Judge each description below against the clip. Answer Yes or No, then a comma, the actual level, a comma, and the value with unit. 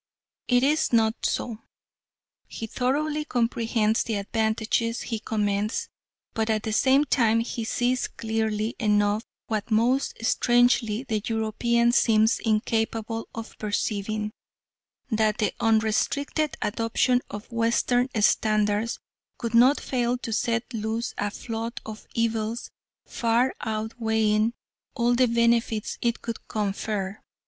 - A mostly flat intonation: Yes, narrow, 1.7 semitones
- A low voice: No, high, 225 Hz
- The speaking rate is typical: No, slow, 120 wpm